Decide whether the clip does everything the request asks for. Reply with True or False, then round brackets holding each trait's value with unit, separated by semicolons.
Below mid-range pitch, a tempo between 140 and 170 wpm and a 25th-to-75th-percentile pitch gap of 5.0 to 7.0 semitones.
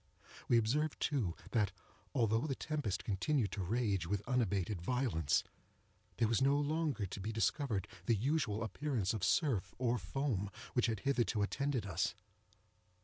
True (115 Hz; 145 wpm; 5.3 semitones)